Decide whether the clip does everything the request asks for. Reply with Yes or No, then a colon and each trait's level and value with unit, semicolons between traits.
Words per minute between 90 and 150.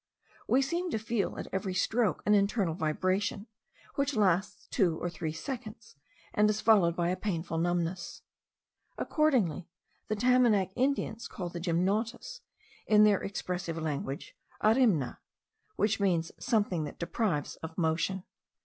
Yes: slow, 135 wpm